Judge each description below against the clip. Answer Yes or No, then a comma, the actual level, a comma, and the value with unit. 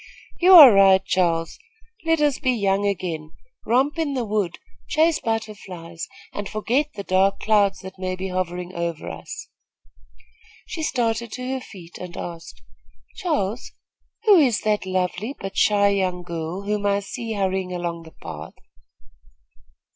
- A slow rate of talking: No, average, 145 wpm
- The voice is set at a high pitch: Yes, high, 195 Hz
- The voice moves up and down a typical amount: Yes, average, 4.5 semitones